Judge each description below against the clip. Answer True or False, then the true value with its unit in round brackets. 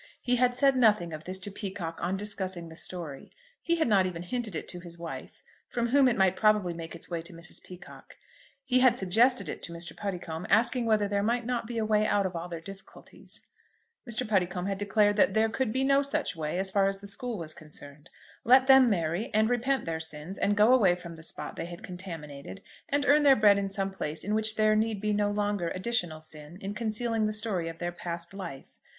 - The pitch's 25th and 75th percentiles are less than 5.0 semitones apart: True (4.5 semitones)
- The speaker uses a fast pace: True (230 wpm)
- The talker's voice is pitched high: True (200 Hz)